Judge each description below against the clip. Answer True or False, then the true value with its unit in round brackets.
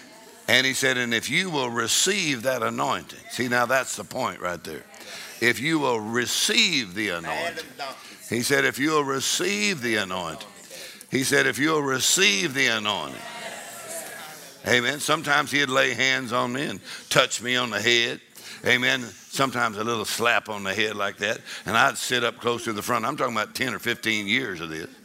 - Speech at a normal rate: True (185 wpm)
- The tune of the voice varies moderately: True (3.1 semitones)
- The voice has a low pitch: True (125 Hz)